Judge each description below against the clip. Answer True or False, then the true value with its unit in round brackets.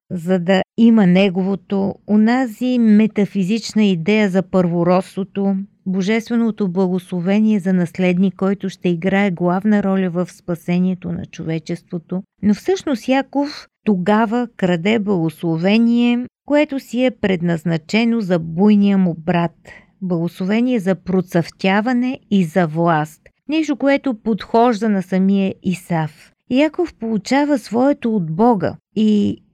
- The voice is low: False (195 Hz)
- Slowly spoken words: True (110 wpm)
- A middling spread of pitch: True (3.7 semitones)